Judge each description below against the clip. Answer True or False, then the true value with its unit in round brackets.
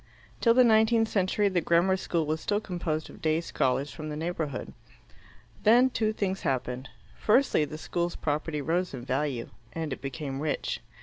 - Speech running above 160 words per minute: True (170 wpm)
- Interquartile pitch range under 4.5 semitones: False (5.3 semitones)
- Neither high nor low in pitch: True (165 Hz)